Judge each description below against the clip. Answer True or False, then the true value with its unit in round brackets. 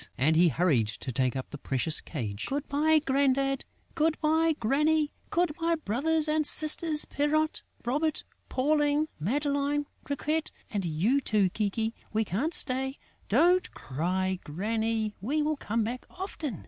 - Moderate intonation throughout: False (7.9 semitones)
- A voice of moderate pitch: False (270 Hz)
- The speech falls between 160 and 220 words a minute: False (145 wpm)